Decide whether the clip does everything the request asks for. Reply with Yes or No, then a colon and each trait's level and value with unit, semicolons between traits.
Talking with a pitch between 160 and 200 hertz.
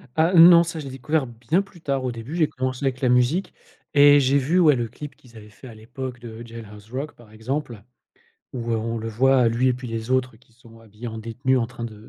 No: low, 125 Hz